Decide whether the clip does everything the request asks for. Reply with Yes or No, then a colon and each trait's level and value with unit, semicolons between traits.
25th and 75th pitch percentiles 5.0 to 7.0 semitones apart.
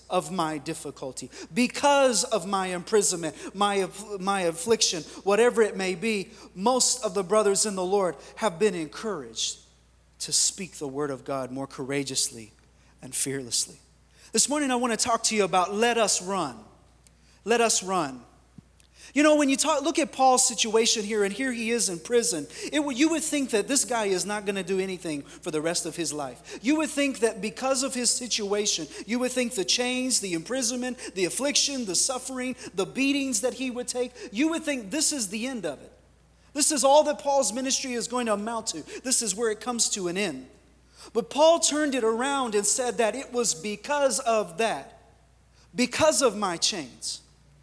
Yes: wide, 5.5 semitones